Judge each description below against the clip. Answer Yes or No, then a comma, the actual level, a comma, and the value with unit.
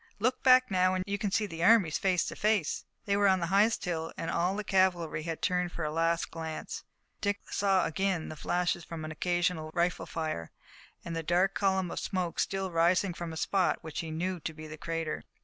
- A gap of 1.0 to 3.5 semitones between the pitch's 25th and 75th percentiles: Yes, average, 2.8 semitones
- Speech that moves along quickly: Yes, fast, 215 wpm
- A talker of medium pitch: Yes, medium, 175 Hz